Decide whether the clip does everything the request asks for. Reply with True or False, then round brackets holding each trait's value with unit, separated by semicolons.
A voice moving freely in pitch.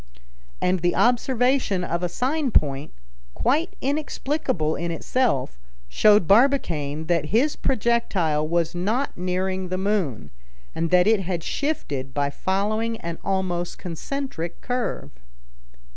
True (6.5 semitones)